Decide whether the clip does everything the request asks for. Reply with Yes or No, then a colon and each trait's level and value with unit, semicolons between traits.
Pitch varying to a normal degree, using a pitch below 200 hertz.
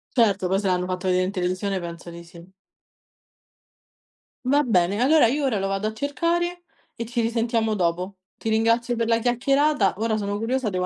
No: average, 4.7 semitones; high, 220 Hz